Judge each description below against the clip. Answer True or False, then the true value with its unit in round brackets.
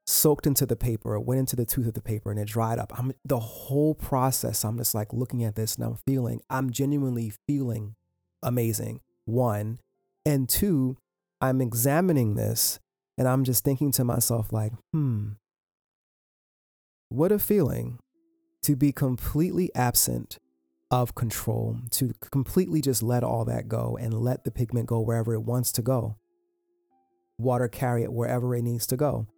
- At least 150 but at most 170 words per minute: True (165 wpm)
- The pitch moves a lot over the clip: False (3.3 semitones)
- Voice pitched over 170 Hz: False (120 Hz)